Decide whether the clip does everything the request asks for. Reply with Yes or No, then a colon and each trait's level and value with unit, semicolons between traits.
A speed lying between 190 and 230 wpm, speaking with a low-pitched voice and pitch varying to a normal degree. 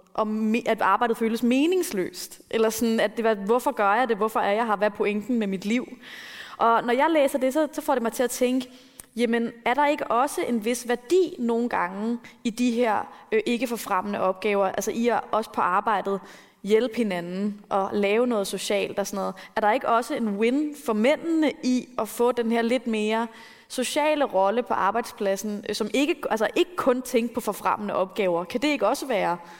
No: average, 205 wpm; high, 230 Hz; average, 3.2 semitones